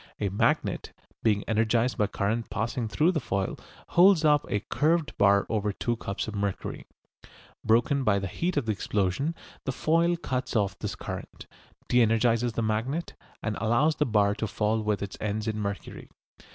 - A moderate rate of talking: Yes, average, 180 wpm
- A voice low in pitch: Yes, low, 110 Hz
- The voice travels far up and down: No, average, 4.3 semitones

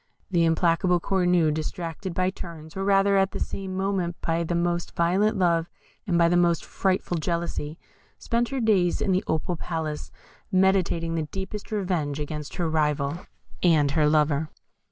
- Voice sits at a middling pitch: Yes, medium, 170 Hz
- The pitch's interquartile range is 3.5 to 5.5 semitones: No, average, 3.0 semitones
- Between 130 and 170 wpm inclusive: Yes, average, 160 wpm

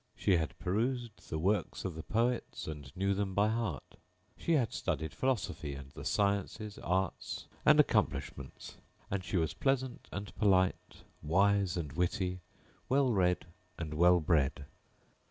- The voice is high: No, very low, 95 Hz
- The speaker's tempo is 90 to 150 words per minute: Yes, average, 145 wpm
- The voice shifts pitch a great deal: No, average, 4.5 semitones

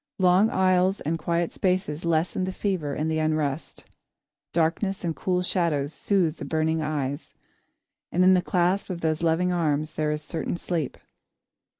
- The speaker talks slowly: No, average, 160 wpm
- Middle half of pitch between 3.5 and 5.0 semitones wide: No, average, 2.7 semitones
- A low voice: No, medium, 170 Hz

